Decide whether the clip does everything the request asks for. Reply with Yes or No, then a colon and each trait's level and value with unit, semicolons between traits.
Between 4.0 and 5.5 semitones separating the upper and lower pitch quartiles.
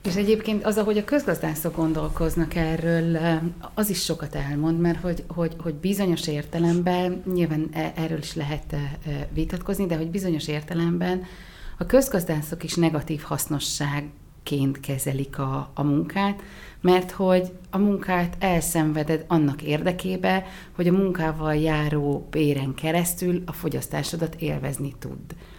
No: average, 3.1 semitones